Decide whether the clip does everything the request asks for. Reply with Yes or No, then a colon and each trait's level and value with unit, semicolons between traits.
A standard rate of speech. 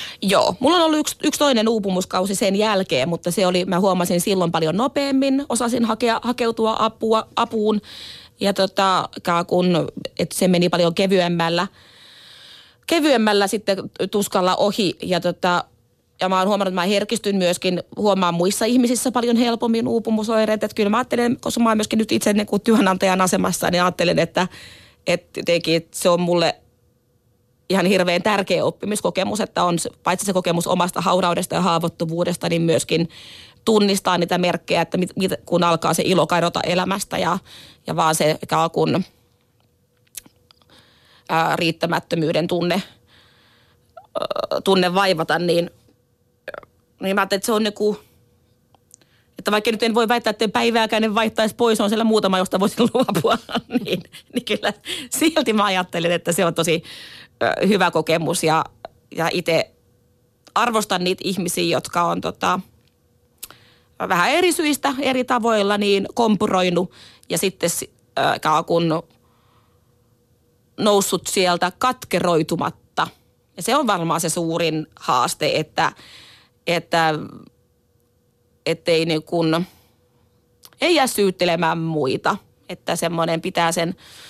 Yes: average, 130 wpm